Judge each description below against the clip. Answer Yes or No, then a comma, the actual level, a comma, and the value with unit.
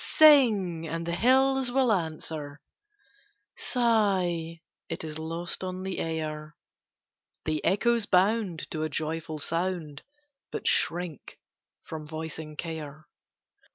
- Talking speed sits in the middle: No, slow, 110 wpm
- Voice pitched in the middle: Yes, medium, 165 Hz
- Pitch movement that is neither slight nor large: Yes, average, 4.2 semitones